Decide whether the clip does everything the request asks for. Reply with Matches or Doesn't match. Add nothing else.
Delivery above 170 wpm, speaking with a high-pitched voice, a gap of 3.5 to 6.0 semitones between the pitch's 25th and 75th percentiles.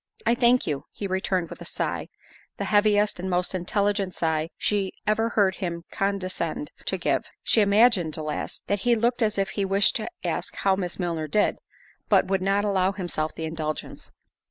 Doesn't match